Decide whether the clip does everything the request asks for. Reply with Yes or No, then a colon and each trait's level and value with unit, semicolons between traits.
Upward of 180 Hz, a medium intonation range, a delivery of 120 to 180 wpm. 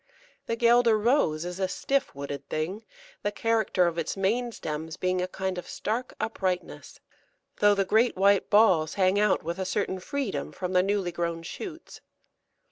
Yes: high, 190 Hz; average, 4.1 semitones; average, 170 wpm